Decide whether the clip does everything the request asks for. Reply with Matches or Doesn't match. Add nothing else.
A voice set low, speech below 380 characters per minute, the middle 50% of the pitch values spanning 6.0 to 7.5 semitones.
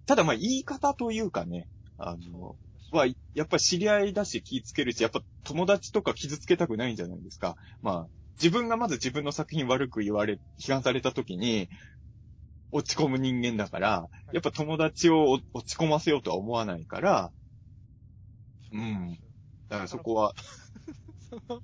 Matches